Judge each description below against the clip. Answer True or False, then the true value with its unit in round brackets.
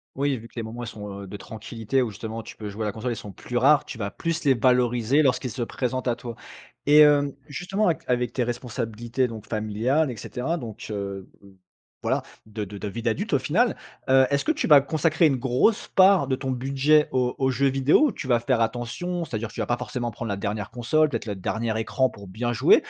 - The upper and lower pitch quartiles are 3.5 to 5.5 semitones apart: True (3.8 semitones)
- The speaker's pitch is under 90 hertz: False (120 Hz)